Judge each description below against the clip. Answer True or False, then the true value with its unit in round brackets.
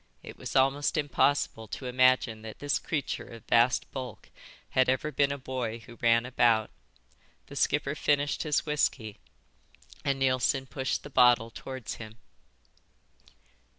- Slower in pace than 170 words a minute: True (140 wpm)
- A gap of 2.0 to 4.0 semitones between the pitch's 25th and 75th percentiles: True (3.2 semitones)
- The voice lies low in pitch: True (130 Hz)